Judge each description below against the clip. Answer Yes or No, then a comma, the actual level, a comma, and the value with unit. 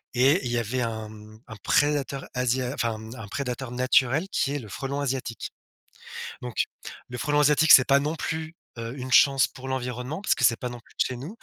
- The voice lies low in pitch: Yes, low, 130 Hz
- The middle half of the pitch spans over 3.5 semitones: No, average, 3.0 semitones